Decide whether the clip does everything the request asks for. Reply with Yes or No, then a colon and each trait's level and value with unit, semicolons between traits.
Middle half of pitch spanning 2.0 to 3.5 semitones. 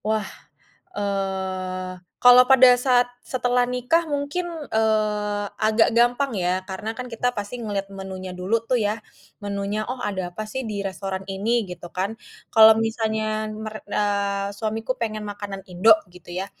Yes: average, 3.0 semitones